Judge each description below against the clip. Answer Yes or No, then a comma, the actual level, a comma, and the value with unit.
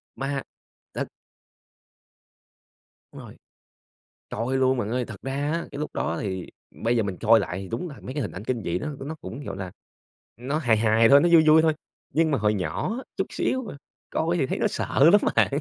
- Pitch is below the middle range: Yes, low, 130 Hz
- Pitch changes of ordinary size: No, wide, 6.1 semitones